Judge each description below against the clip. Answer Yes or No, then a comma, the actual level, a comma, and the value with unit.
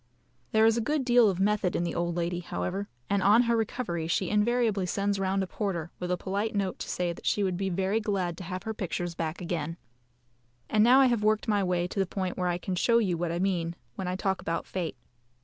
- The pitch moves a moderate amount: Yes, average, 3.2 semitones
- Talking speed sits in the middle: No, fast, 245 wpm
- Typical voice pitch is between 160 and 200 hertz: Yes, high, 190 Hz